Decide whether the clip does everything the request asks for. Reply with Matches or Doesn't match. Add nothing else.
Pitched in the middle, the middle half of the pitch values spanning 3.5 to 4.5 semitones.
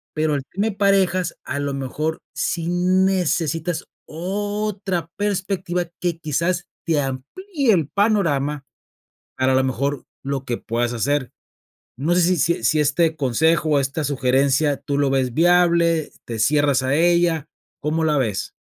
Matches